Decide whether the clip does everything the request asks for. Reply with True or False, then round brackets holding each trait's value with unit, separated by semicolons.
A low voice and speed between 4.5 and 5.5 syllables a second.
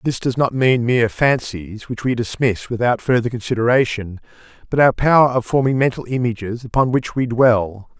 True (120 Hz; 5.2 syllables/s)